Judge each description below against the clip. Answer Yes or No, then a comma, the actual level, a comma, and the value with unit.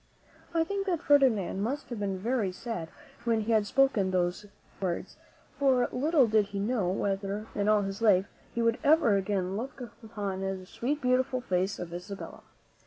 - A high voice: Yes, high, 210 Hz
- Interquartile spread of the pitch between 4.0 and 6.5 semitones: Yes, average, 4.6 semitones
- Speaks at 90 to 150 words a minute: No, average, 175 wpm